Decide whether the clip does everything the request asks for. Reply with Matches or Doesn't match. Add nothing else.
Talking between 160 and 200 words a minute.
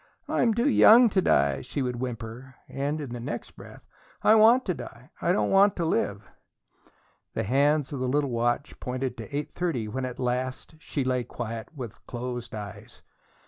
Matches